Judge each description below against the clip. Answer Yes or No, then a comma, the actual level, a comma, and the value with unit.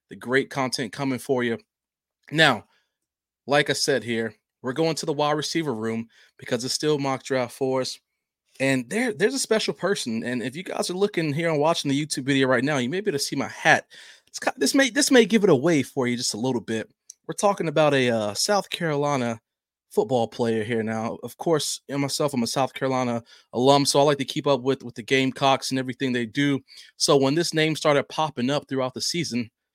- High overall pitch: No, low, 135 Hz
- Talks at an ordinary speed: No, fast, 230 wpm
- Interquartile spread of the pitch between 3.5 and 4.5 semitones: Yes, average, 4.0 semitones